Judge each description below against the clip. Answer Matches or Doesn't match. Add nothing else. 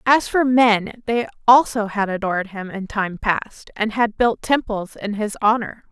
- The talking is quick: Doesn't match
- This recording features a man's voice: Doesn't match